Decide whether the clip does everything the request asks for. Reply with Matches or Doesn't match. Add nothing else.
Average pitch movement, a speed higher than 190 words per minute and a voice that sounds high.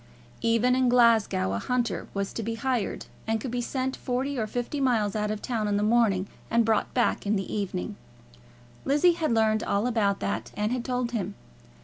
Matches